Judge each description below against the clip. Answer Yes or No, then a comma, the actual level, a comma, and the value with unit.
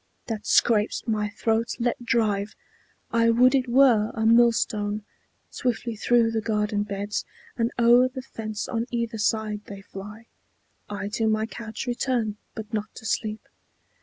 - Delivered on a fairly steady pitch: Yes, narrow, 2.0 semitones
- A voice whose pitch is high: Yes, high, 225 Hz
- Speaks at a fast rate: No, average, 150 wpm